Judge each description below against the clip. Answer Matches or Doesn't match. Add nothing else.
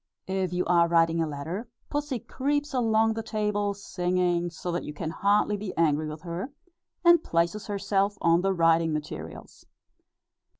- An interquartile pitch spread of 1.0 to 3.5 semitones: Doesn't match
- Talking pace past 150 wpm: Matches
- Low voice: Doesn't match